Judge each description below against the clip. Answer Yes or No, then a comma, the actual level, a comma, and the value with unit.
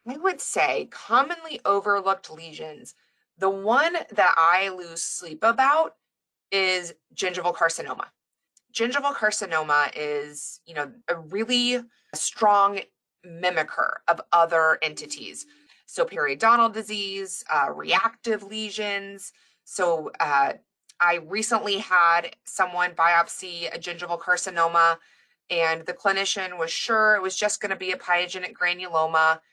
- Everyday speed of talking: No, slow, 120 wpm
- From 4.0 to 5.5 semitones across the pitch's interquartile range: Yes, average, 4.7 semitones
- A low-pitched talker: No, high, 190 Hz